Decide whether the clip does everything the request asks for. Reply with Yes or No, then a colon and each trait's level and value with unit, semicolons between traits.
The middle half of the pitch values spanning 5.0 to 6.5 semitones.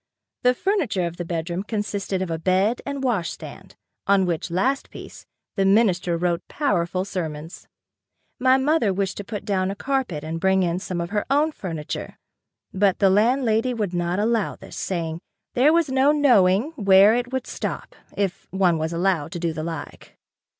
Yes: wide, 5.6 semitones